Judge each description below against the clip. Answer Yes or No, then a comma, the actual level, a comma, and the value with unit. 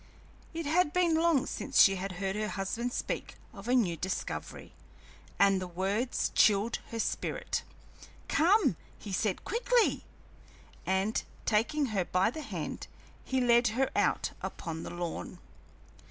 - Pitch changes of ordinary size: No, wide, 6.9 semitones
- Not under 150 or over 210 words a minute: No, average, 140 wpm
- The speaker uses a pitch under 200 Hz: No, high, 220 Hz